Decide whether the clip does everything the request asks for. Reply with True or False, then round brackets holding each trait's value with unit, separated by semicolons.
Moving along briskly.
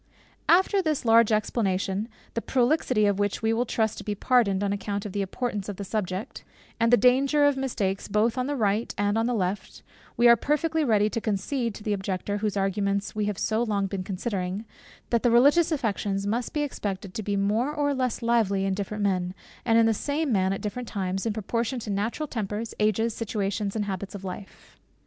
True (210 wpm)